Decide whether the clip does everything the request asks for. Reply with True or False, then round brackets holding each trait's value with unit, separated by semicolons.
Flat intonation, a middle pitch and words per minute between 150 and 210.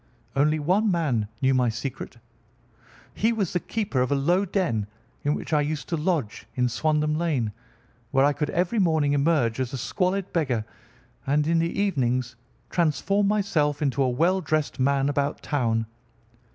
False (4.5 semitones; 150 Hz; 165 wpm)